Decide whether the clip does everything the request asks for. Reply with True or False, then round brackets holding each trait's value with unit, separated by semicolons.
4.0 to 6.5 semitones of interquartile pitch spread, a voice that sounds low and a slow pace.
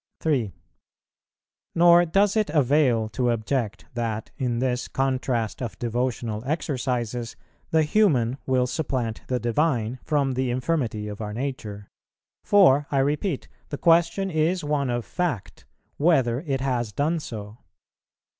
True (4.5 semitones; 130 Hz; 130 wpm)